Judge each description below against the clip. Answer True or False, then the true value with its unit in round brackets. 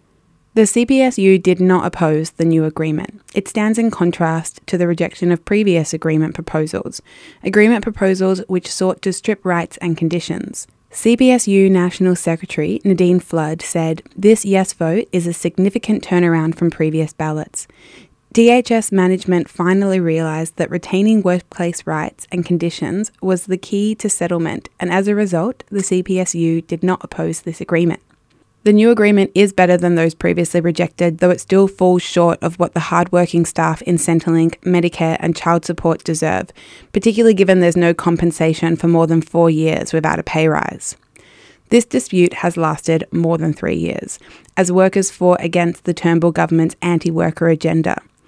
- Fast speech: False (160 wpm)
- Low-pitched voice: False (175 Hz)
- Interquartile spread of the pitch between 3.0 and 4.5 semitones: False (2.5 semitones)